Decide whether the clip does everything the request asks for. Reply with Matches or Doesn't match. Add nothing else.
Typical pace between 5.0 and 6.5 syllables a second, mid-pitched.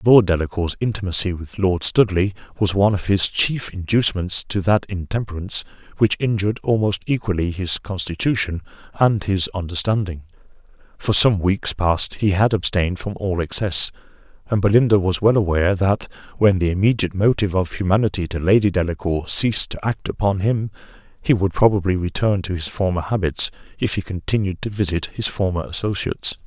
Doesn't match